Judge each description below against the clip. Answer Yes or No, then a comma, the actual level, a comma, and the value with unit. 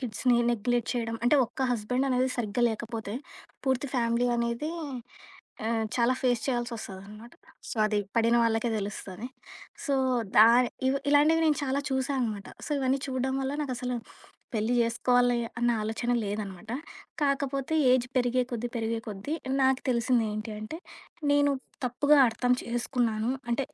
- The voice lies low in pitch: No, high, 240 Hz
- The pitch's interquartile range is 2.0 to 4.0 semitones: Yes, narrow, 2.5 semitones